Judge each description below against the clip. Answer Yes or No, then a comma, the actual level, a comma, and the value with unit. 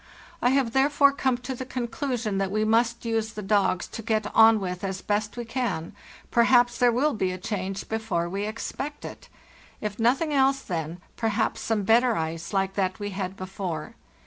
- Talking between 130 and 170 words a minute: No, average, 180 wpm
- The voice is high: Yes, high, 220 Hz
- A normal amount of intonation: Yes, average, 4.0 semitones